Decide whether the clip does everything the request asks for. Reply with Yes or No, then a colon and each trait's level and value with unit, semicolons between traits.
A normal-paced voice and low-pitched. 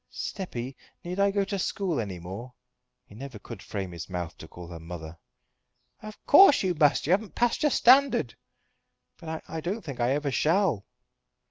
No: average, 180 wpm; medium, 145 Hz